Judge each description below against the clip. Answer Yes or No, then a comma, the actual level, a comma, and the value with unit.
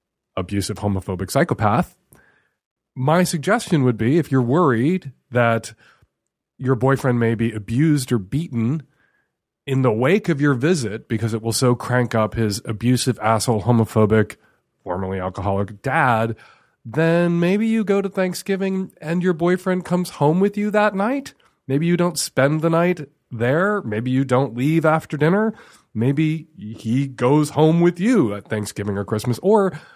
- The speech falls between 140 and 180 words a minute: Yes, average, 150 wpm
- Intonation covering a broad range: Yes, wide, 7.1 semitones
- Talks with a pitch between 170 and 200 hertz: No, low, 135 Hz